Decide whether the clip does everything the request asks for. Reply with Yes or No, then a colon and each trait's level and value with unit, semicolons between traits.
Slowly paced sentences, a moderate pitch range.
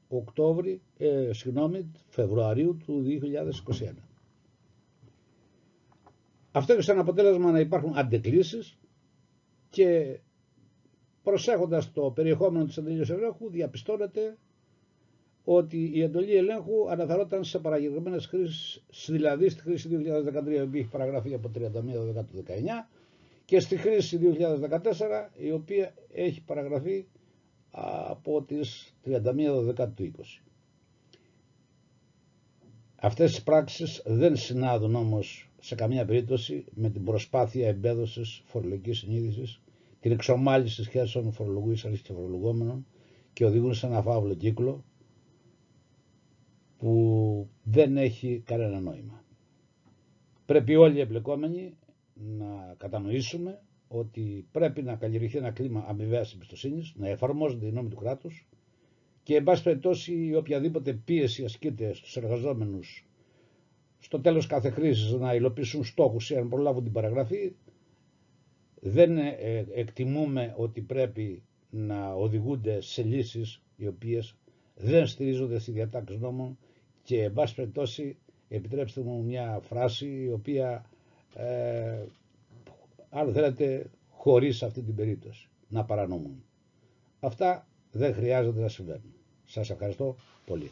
Yes: slow, 110 wpm; average, 5.0 semitones